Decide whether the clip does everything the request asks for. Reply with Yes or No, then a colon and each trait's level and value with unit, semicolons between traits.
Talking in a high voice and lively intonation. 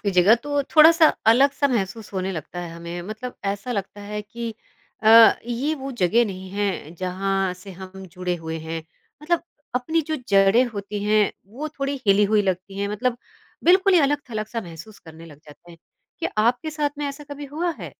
Yes: high, 210 Hz; wide, 6.3 semitones